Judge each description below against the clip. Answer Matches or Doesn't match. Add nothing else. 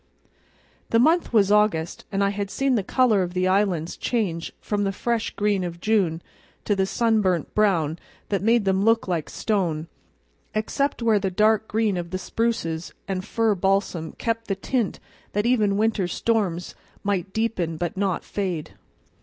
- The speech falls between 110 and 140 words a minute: Doesn't match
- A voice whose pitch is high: Matches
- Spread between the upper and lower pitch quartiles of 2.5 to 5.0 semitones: Matches